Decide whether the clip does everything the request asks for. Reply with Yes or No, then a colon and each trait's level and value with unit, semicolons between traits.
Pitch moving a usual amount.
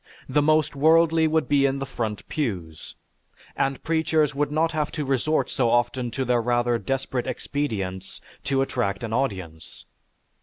Yes: average, 4.3 semitones